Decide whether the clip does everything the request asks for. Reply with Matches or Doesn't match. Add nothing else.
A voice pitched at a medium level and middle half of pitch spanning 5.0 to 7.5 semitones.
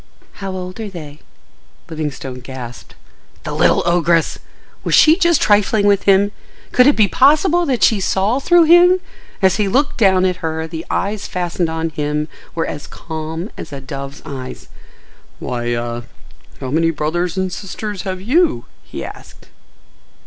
Matches